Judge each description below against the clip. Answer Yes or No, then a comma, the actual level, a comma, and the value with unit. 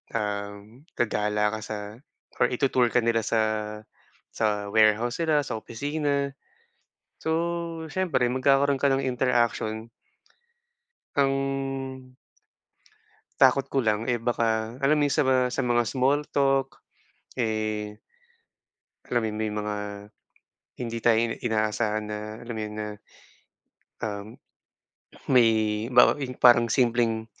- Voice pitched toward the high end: No, low, 120 Hz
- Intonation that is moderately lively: Yes, average, 3.8 semitones